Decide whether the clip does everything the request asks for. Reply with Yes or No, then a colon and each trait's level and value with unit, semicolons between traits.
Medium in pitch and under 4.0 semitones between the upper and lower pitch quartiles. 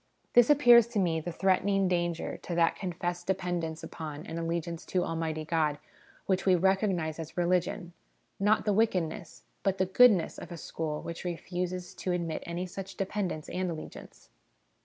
Yes: medium, 175 Hz; narrow, 2.6 semitones